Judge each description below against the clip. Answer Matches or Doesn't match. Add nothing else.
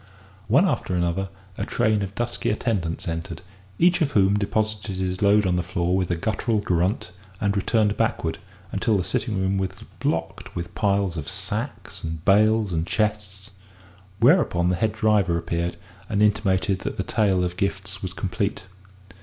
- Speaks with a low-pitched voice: Matches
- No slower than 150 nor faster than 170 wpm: Matches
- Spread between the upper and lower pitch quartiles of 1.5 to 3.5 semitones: Matches